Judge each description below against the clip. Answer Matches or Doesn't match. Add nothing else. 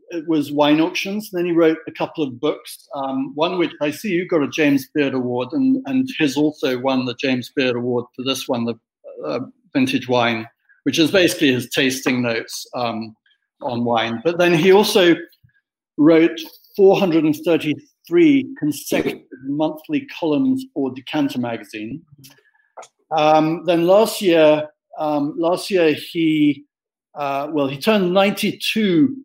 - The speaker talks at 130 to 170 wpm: Matches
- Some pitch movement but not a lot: Doesn't match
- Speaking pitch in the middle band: Matches